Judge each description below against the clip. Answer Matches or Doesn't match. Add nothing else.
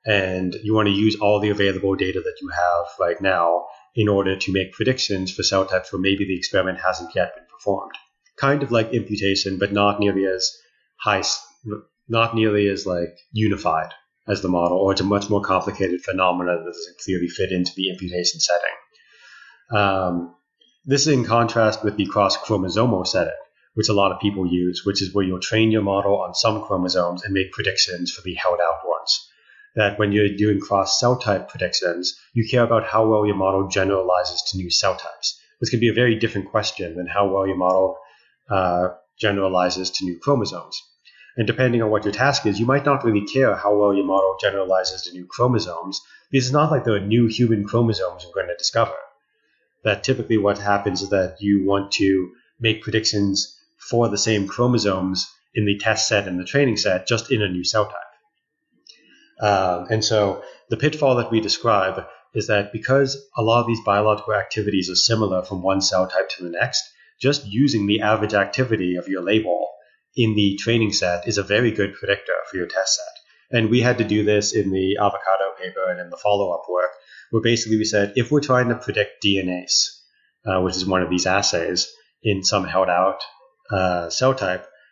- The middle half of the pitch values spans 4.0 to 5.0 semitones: Doesn't match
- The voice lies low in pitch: Matches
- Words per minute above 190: Matches